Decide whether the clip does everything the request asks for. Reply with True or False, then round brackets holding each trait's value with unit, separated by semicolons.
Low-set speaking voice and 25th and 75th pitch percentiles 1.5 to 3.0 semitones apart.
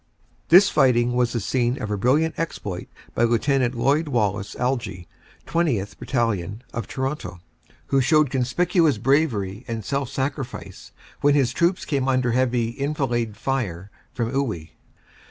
False (125 Hz; 3.6 semitones)